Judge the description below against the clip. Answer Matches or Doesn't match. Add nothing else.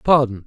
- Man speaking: Doesn't match